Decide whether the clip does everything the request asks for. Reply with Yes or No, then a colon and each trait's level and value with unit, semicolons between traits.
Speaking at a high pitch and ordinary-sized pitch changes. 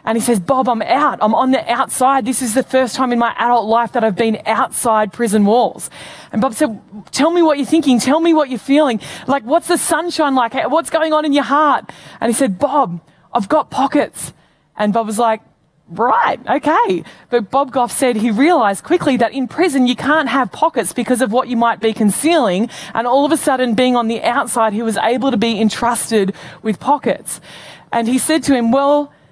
Yes: very high, 250 Hz; average, 3.9 semitones